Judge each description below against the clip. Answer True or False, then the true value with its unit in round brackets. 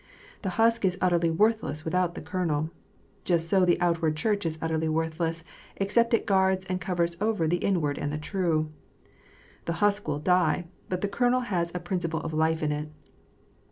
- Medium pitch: True (175 Hz)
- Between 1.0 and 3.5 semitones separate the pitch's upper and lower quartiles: True (2.9 semitones)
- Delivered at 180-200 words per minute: True (185 wpm)